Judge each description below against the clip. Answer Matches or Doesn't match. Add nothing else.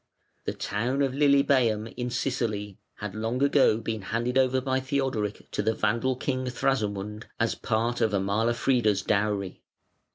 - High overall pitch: Doesn't match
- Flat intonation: Doesn't match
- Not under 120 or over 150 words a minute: Matches